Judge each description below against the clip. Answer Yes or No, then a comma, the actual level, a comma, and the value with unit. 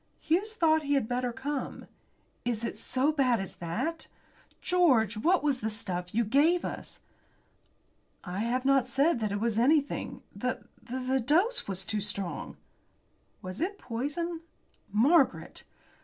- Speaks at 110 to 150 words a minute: Yes, average, 145 wpm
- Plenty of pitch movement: Yes, wide, 6.1 semitones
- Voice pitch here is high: Yes, very high, 260 Hz